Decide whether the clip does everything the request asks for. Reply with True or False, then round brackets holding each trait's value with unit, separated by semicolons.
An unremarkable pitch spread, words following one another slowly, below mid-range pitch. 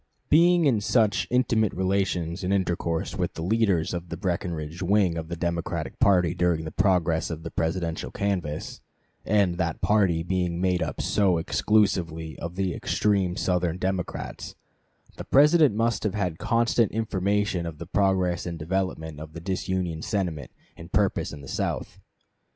False (3.3 semitones; 160 wpm; 90 Hz)